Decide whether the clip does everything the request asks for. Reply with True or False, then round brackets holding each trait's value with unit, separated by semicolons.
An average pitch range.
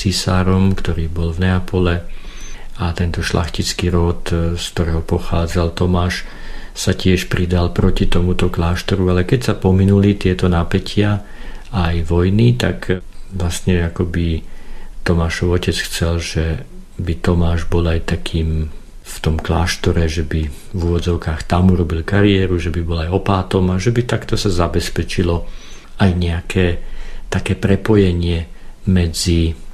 False (2.1 semitones)